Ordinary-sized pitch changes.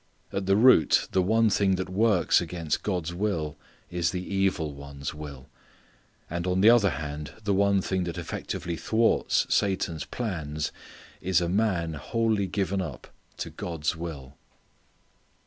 Yes: average, 4.0 semitones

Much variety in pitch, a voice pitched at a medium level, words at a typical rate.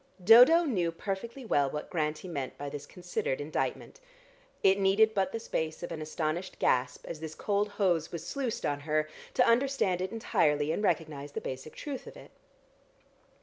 Yes: wide, 5.8 semitones; medium, 175 Hz; average, 175 wpm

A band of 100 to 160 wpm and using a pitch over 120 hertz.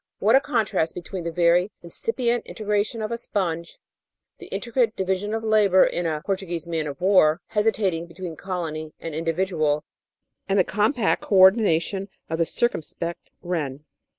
Yes: average, 155 wpm; medium, 185 Hz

